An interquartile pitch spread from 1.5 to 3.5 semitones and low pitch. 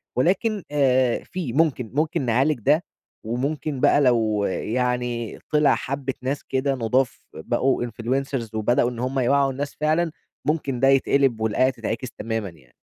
Yes: average, 3.1 semitones; low, 130 Hz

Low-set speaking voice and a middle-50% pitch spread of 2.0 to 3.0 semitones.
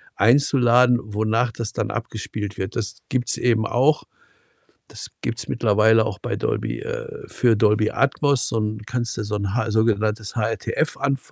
Yes: low, 115 Hz; narrow, 2.4 semitones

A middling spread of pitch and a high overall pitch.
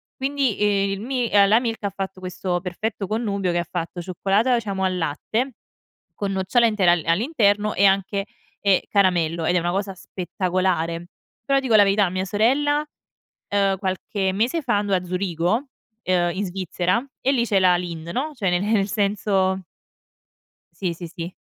Yes: average, 3.1 semitones; high, 195 Hz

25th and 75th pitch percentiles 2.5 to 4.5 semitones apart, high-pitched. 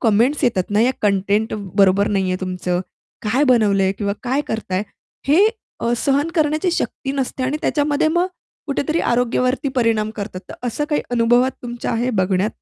No: wide, 5.5 semitones; high, 235 Hz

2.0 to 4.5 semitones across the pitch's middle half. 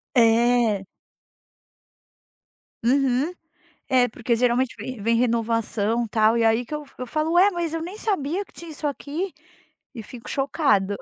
No: average, 4.9 semitones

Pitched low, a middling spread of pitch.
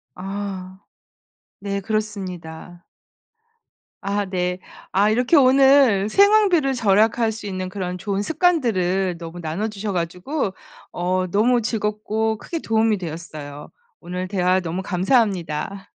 No: high, 200 Hz; average, 3.5 semitones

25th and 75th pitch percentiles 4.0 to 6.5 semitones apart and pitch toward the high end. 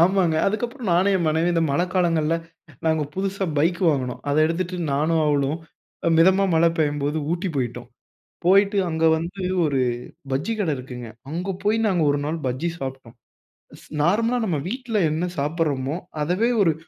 No: average, 4.3 semitones; medium, 165 Hz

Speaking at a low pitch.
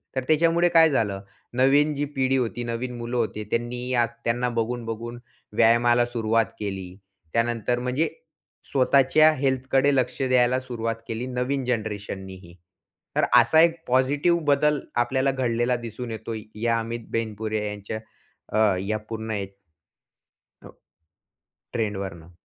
Yes: low, 120 Hz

